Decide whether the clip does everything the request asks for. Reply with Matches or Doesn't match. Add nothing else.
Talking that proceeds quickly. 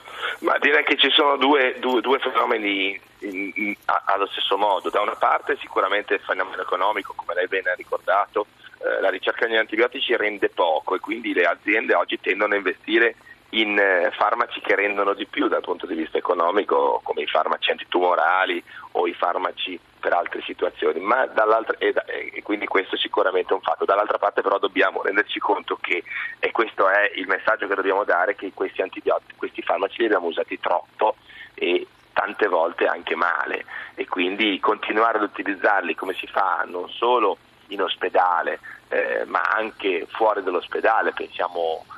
Matches